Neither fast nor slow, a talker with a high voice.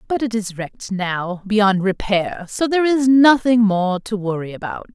Yes: average, 180 wpm; high, 210 Hz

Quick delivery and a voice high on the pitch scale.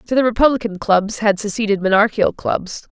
No: average, 160 wpm; high, 210 Hz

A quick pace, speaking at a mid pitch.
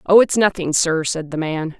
Yes: fast, 235 wpm; medium, 170 Hz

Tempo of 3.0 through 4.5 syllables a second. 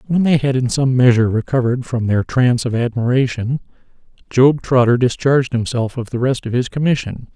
No: 5.8 syllables/s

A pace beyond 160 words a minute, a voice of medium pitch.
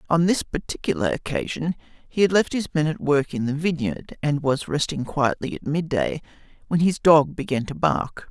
Yes: average, 190 wpm; medium, 150 Hz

